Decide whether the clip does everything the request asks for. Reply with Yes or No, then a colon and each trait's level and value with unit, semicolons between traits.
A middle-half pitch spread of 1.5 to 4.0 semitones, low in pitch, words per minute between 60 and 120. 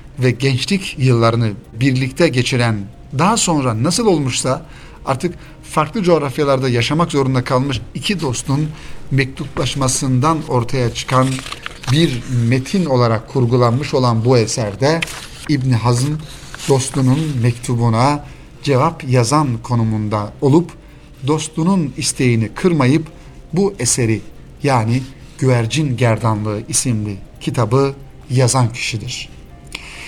Yes: average, 3.7 semitones; low, 130 Hz; slow, 95 wpm